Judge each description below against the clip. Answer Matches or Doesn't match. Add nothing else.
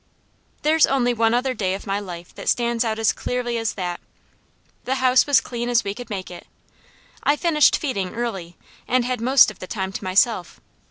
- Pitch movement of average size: Matches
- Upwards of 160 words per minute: Matches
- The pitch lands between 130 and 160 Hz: Doesn't match